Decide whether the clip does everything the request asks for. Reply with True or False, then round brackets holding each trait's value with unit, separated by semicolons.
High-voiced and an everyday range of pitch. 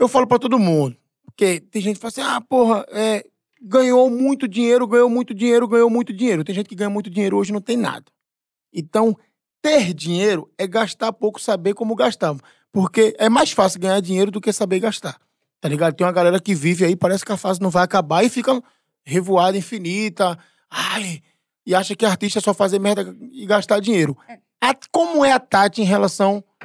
True (210 Hz; 3.9 semitones)